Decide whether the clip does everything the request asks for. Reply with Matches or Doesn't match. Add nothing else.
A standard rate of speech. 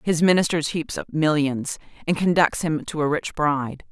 Matches